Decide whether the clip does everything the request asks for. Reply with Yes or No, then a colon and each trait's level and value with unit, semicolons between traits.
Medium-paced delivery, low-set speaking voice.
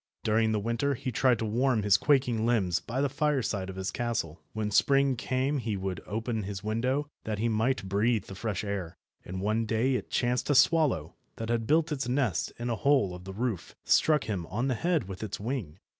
No: fast, 215 wpm; low, 115 Hz